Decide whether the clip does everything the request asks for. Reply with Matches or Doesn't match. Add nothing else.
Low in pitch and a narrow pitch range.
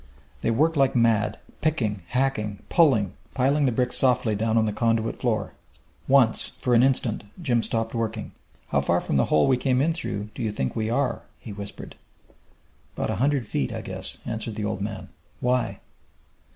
Doesn't match